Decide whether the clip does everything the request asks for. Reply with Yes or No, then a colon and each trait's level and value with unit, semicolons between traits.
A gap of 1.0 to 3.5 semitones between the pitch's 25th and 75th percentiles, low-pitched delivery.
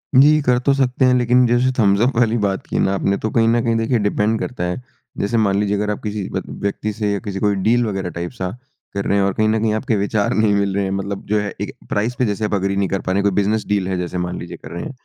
Yes: average, 2.8 semitones; low, 105 Hz